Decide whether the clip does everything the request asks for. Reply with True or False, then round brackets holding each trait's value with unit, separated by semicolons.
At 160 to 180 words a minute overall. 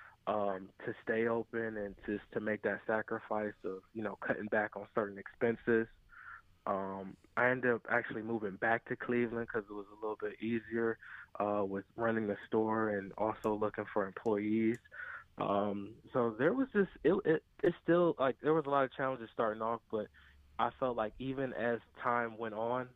False (190 wpm)